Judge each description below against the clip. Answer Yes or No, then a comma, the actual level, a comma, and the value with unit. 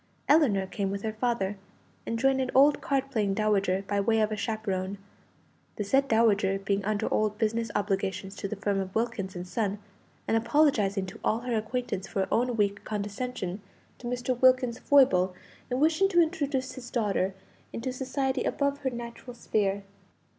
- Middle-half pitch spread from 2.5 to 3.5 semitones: No, average, 4.3 semitones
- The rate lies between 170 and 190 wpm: Yes, average, 175 wpm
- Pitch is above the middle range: Yes, high, 220 Hz